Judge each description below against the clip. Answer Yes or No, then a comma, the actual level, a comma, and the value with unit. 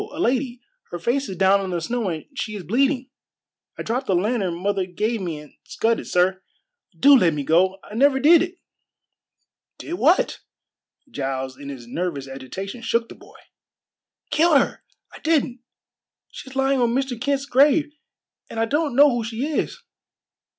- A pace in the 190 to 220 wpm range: No, average, 170 wpm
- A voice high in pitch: Yes, high, 230 Hz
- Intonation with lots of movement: Yes, wide, 7.1 semitones